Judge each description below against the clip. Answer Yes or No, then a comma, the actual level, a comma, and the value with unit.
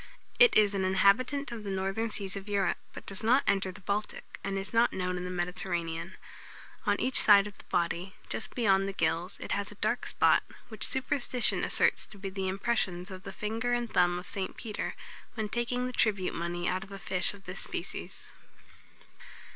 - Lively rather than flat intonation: No, average, 2.8 semitones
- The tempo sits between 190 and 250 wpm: Yes, average, 200 wpm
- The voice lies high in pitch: Yes, high, 195 Hz